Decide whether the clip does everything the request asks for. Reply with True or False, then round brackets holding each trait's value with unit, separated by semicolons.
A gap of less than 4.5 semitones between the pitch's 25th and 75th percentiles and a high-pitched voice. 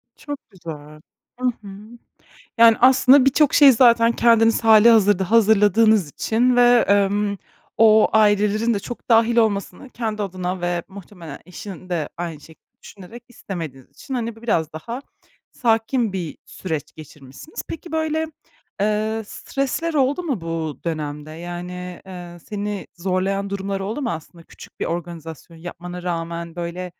False (5.0 semitones; 200 Hz)